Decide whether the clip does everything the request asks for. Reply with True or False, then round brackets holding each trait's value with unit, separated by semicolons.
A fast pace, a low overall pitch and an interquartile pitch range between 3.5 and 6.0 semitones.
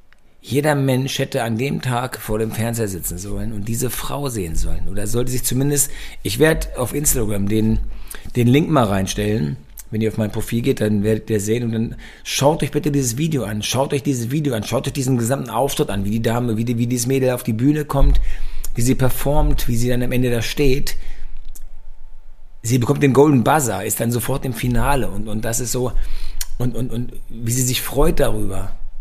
True (215 wpm; 120 Hz; 3.8 semitones)